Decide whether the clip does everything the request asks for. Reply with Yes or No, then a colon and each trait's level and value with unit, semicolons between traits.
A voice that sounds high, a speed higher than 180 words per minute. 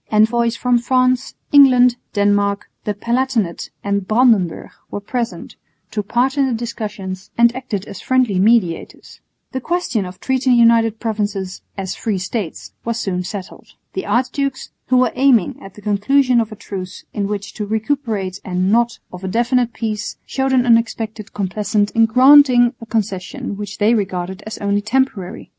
No: high, 220 Hz; average, 160 wpm